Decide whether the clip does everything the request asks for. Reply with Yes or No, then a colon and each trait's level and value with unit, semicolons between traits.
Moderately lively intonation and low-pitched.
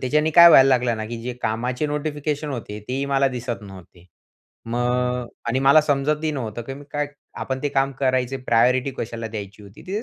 Yes: average, 3.4 semitones; low, 130 Hz